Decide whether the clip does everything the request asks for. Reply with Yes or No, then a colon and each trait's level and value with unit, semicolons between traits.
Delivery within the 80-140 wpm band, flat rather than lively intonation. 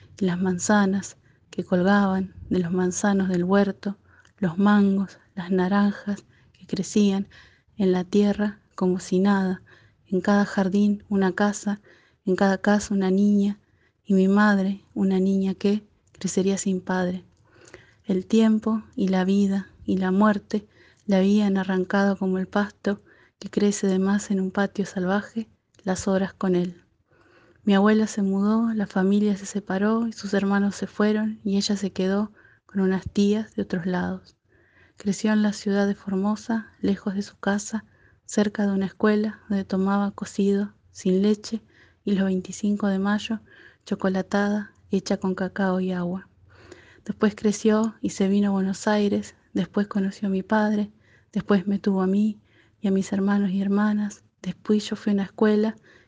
No: average, 160 wpm; narrow, 1.5 semitones